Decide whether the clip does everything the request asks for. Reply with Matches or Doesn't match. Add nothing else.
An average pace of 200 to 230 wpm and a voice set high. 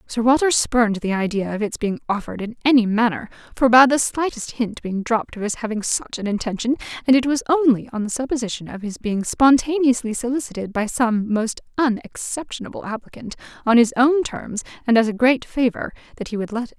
Matches